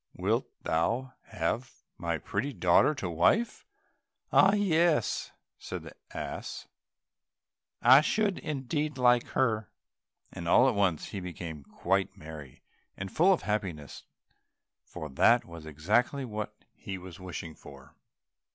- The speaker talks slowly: Yes, slow, 125 wpm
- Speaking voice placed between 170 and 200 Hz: No, low, 105 Hz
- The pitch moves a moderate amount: No, wide, 8.0 semitones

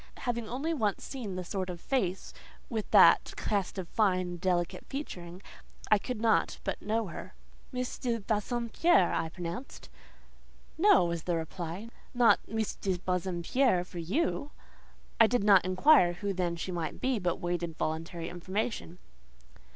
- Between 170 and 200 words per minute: No, average, 150 wpm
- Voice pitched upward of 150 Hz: Yes, high, 190 Hz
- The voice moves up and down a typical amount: Yes, average, 4.9 semitones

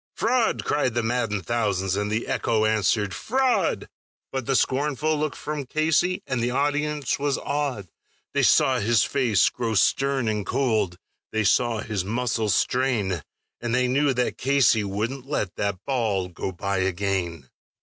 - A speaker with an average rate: Yes, average, 155 wpm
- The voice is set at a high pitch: No, low, 120 Hz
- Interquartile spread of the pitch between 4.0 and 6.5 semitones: Yes, average, 5.1 semitones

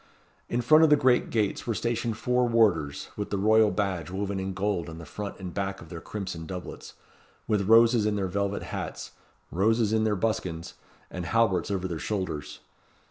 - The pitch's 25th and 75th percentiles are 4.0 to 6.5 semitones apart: No, average, 3.4 semitones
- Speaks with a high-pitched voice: No, low, 100 Hz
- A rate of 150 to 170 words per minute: No, average, 190 wpm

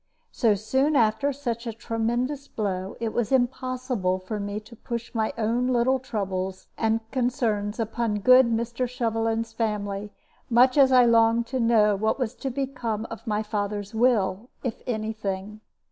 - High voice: Yes, high, 225 Hz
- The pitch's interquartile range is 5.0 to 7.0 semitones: No, average, 2.9 semitones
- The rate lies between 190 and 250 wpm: No, average, 160 wpm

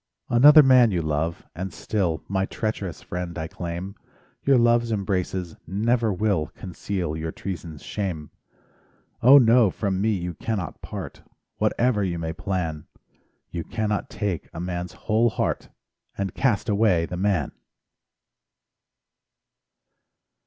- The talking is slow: Yes, slow, 125 wpm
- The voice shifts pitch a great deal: No, average, 4.3 semitones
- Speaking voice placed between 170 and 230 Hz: No, very low, 95 Hz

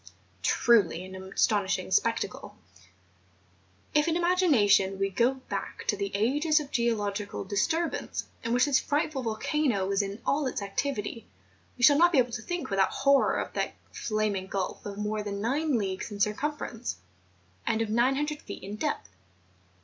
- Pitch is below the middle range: No, high, 230 Hz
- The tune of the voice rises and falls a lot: Yes, wide, 6.1 semitones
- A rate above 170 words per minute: No, average, 160 wpm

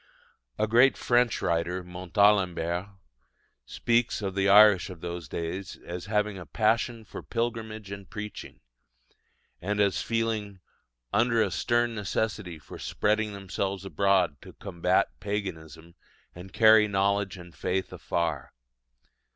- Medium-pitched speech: No, low, 100 Hz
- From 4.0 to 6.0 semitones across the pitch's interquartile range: No, average, 3.2 semitones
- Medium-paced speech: No, slow, 125 wpm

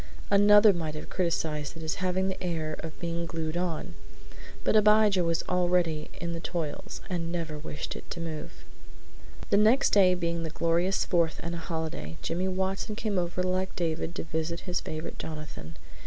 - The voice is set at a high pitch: No, medium, 170 Hz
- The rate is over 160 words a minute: Yes, average, 175 wpm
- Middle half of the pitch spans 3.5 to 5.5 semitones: No, narrow, 2.6 semitones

